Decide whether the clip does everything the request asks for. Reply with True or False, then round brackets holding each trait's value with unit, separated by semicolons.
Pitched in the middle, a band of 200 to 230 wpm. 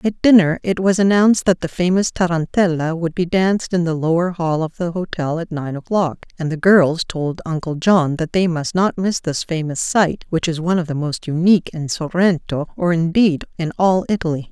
True (170 Hz; 205 wpm)